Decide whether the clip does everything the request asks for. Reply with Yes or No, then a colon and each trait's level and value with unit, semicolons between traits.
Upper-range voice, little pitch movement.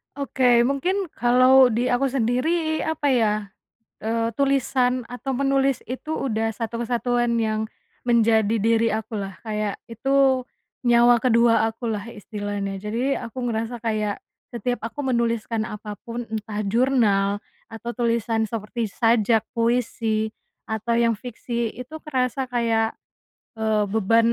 Yes: high, 235 Hz; narrow, 2.3 semitones